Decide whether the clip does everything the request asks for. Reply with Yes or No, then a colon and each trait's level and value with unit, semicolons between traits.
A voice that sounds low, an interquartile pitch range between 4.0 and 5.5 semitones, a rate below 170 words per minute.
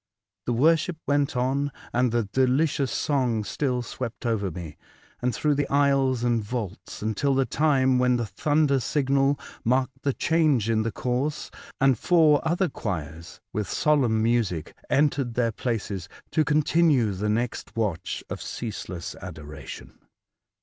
Yes: low, 125 Hz; average, 4.4 semitones; average, 145 wpm